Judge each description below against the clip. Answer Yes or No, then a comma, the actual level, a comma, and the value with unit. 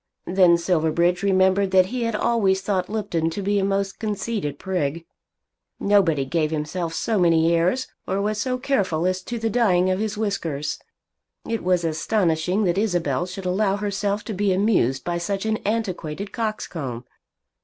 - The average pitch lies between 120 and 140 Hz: No, high, 190 Hz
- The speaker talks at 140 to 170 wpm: Yes, average, 165 wpm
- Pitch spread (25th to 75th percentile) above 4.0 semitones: No, average, 3.6 semitones